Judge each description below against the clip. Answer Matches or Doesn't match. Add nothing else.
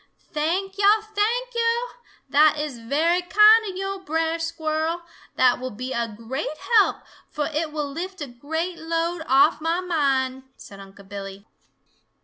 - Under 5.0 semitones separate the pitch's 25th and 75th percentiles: Doesn't match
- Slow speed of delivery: Doesn't match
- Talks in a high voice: Matches